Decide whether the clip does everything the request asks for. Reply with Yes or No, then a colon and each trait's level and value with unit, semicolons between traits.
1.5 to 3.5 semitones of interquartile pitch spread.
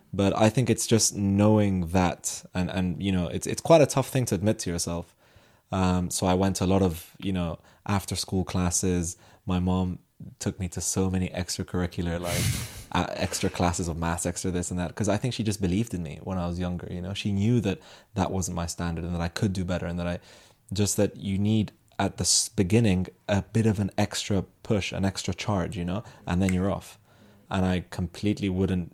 Yes: narrow, 2.6 semitones